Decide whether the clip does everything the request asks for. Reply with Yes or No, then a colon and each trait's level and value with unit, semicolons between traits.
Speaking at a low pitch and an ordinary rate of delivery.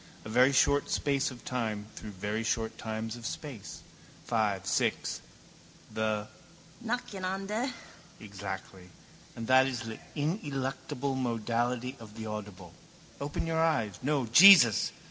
No: low, 120 Hz; slow, 125 wpm